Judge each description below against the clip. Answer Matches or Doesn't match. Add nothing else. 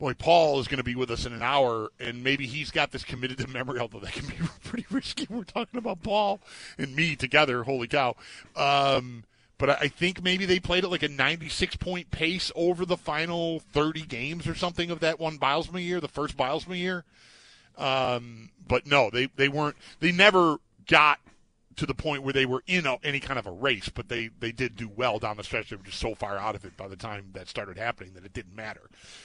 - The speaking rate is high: Matches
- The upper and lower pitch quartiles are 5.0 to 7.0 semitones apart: Matches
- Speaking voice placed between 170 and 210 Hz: Doesn't match